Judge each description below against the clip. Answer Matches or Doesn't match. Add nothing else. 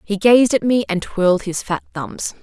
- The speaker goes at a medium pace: Doesn't match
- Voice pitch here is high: Matches